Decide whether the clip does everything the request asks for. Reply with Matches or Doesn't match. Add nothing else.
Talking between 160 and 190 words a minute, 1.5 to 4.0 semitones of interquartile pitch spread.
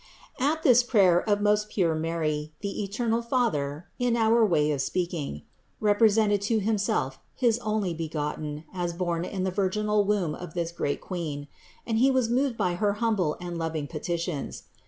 Doesn't match